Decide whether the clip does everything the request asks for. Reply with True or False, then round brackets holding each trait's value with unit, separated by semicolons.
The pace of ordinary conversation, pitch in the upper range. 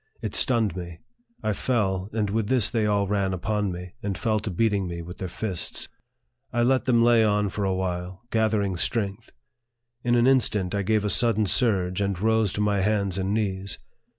False (195 wpm; 105 Hz)